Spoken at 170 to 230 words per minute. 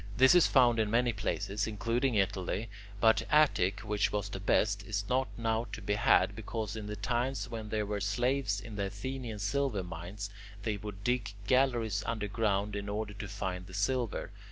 Yes: average, 180 wpm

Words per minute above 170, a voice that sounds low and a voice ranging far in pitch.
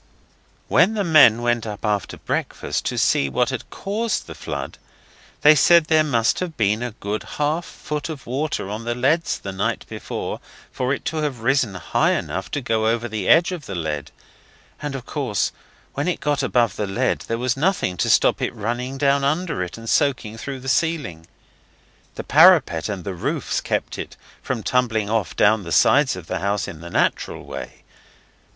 Yes: average, 190 wpm; low, 120 Hz; wide, 6.0 semitones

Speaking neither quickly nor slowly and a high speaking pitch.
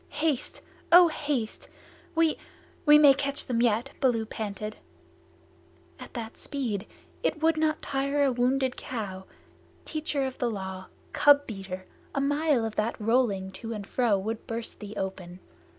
Yes: average, 150 wpm; high, 240 Hz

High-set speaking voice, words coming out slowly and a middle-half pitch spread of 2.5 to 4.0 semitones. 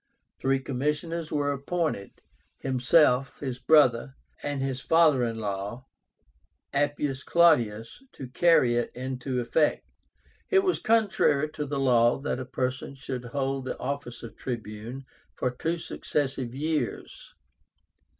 No: low, 135 Hz; slow, 125 wpm; average, 3.2 semitones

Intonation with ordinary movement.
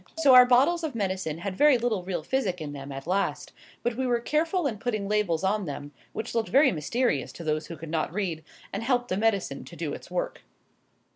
No: wide, 7.0 semitones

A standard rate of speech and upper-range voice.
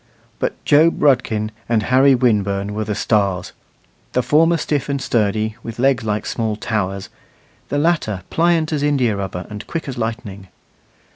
No: average, 150 wpm; low, 115 Hz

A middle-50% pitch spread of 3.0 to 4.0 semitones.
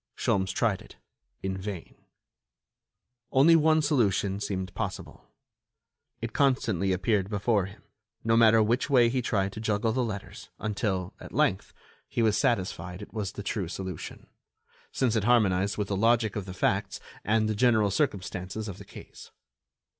Yes: average, 3.3 semitones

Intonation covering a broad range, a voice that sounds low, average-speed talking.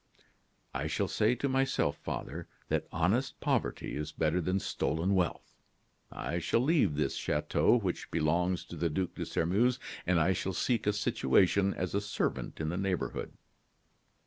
No: average, 3.8 semitones; very low, 90 Hz; average, 160 wpm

